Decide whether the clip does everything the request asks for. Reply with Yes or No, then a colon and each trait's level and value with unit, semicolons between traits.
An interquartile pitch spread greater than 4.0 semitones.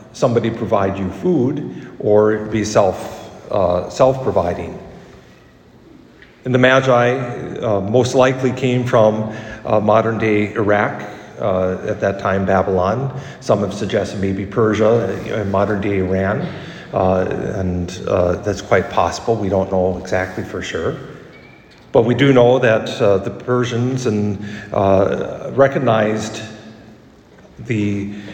No: average, 3.5 semitones